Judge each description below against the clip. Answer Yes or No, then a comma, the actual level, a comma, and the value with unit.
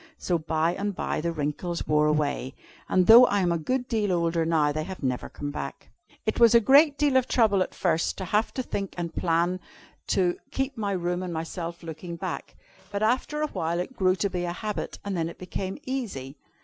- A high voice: No, medium, 180 Hz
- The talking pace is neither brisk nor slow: No, fast, 215 wpm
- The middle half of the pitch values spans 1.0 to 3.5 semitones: No, average, 4.4 semitones